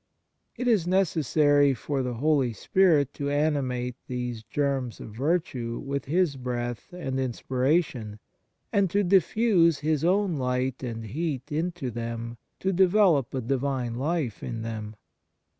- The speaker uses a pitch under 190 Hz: Yes, medium, 140 Hz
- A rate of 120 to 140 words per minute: Yes, slow, 135 wpm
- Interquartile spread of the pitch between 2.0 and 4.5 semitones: No, average, 5.3 semitones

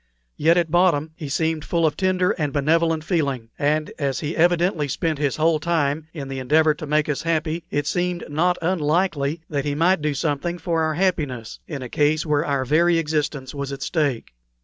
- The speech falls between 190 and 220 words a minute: Yes, average, 195 wpm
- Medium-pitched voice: Yes, medium, 155 Hz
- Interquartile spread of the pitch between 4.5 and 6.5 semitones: No, narrow, 2.6 semitones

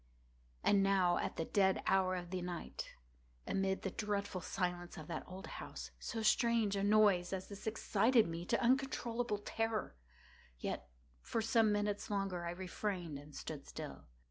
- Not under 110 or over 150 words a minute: No, average, 160 wpm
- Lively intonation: No, average, 3.0 semitones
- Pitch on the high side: Yes, high, 195 Hz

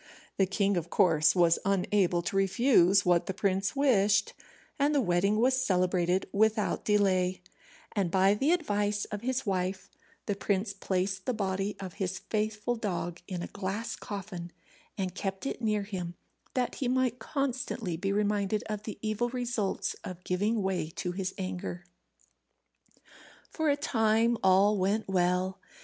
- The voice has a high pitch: Yes, high, 200 Hz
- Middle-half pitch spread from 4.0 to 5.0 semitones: No, average, 2.8 semitones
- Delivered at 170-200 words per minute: No, average, 155 wpm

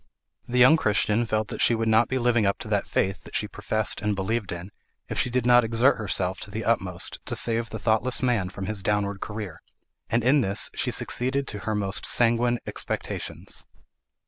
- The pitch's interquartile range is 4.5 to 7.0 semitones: No, average, 3.0 semitones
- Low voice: Yes, low, 110 Hz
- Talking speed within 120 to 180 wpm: No, average, 200 wpm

